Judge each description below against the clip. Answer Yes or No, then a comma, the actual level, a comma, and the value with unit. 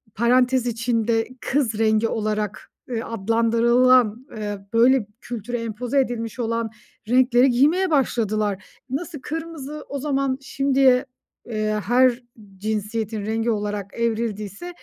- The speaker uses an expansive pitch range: No, average, 3.1 semitones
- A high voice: Yes, high, 235 Hz